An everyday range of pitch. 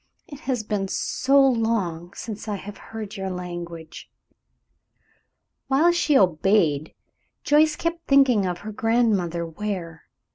No: wide, 6.6 semitones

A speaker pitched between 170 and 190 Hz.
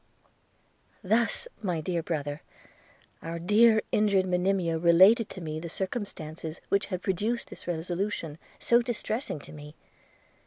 Yes: medium, 185 Hz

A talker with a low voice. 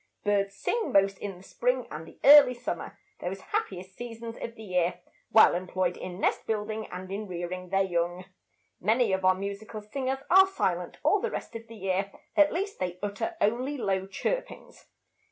No: high, 205 Hz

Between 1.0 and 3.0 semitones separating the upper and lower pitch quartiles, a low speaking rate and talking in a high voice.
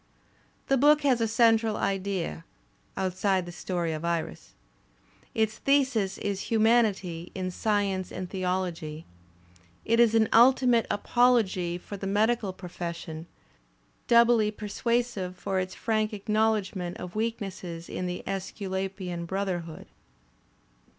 No: average, 3.7 semitones; slow, 115 wpm; high, 195 Hz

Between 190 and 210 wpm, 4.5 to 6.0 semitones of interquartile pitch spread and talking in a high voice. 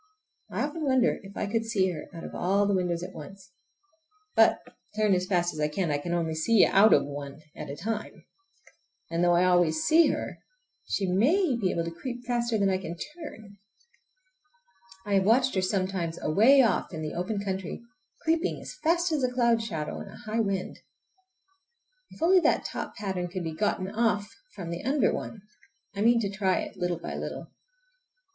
Yes: average, 195 wpm; average, 4.9 semitones; high, 195 Hz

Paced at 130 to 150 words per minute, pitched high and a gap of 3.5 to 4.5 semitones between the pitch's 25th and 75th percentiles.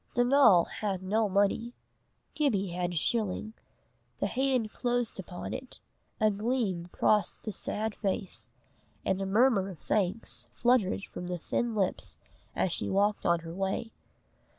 Yes: average, 145 wpm; high, 205 Hz; average, 3.8 semitones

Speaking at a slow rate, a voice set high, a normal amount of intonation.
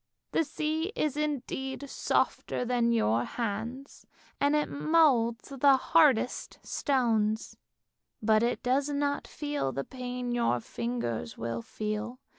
Yes: slow, 120 wpm; very high, 250 Hz; average, 4.8 semitones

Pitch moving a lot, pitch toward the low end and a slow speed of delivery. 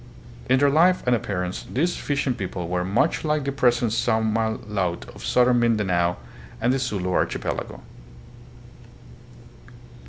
Yes: wide, 5.7 semitones; low, 115 Hz; slow, 130 wpm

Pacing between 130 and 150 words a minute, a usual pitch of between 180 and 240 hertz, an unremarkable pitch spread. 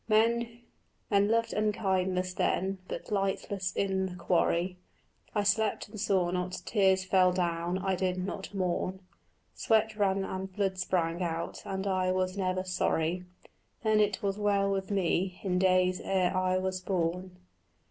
No: average, 145 wpm; high, 190 Hz; narrow, 1.6 semitones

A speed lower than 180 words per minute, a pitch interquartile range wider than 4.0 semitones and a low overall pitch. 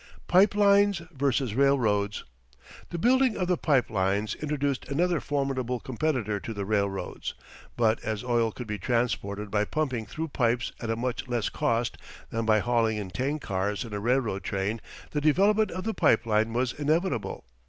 Yes: average, 170 wpm; wide, 5.6 semitones; low, 120 Hz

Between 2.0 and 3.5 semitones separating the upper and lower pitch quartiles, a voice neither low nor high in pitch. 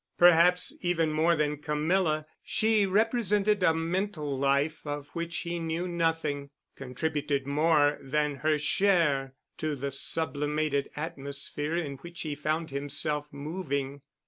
Yes: average, 3.1 semitones; medium, 155 Hz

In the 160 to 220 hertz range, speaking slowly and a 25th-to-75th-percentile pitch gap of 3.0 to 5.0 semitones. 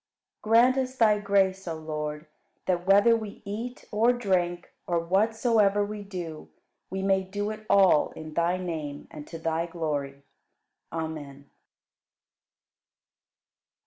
Yes: high, 190 Hz; slow, 130 wpm; average, 4.5 semitones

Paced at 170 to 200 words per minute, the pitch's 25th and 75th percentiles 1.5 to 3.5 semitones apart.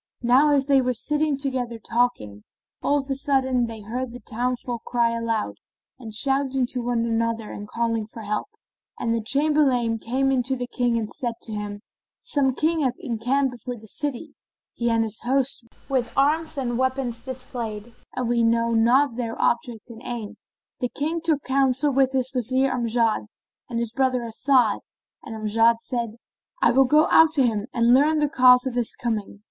Yes: average, 185 wpm; average, 2.8 semitones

